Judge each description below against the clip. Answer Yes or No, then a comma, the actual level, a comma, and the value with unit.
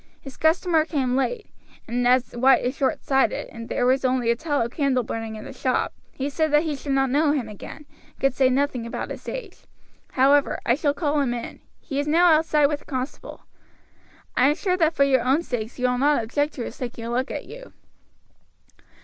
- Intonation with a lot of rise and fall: No, average, 3.2 semitones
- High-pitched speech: Yes, very high, 270 Hz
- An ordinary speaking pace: No, fast, 215 wpm